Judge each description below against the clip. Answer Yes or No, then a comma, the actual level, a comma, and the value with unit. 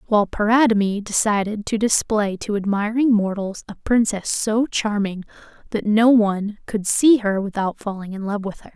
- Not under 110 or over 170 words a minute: Yes, average, 165 wpm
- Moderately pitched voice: No, high, 210 Hz